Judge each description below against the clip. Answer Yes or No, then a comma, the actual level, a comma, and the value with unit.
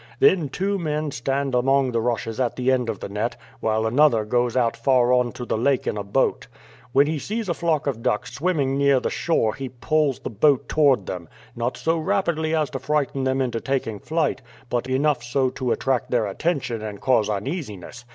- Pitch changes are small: No, average, 4.1 semitones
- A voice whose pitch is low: Yes, low, 130 Hz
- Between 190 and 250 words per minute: Yes, fast, 205 wpm